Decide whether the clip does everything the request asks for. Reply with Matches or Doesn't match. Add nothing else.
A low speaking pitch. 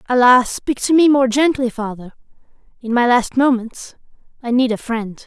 Doesn't match